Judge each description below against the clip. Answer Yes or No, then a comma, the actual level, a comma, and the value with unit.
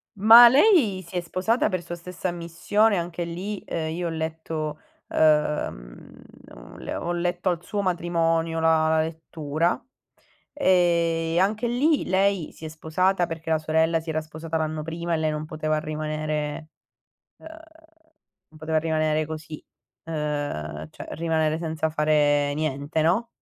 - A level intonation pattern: Yes, narrow, 2.2 semitones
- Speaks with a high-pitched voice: No, medium, 160 Hz